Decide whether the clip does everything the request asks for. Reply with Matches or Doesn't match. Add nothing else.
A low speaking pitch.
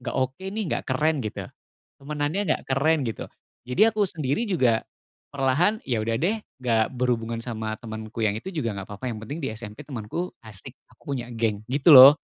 Matches